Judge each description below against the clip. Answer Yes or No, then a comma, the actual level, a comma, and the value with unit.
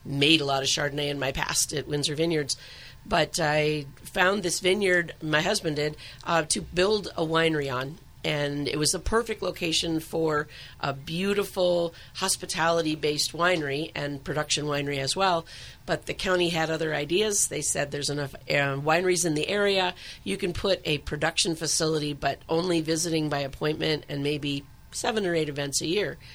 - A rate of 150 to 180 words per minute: Yes, average, 170 wpm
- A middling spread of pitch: Yes, average, 3.2 semitones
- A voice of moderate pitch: Yes, medium, 155 Hz